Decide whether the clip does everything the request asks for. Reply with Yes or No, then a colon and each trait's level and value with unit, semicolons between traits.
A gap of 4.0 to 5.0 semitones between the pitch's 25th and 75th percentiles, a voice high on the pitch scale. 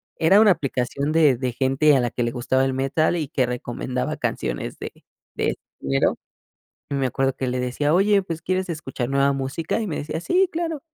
No: average, 4.4 semitones; medium, 140 Hz